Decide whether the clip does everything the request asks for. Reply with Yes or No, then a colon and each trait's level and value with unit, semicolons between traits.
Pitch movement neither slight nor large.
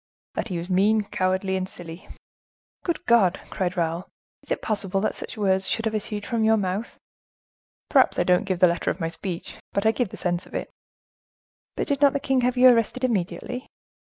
Yes: average, 4.0 semitones